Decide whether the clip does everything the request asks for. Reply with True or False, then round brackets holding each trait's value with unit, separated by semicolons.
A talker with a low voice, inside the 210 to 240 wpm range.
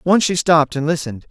False (160 Hz; 230 wpm)